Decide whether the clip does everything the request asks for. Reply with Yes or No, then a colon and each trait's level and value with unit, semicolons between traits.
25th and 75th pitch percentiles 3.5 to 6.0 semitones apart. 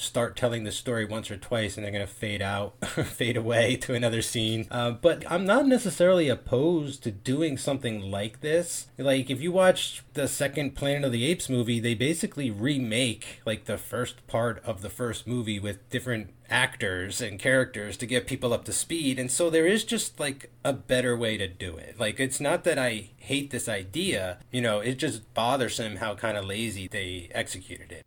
Yes: average, 4.0 semitones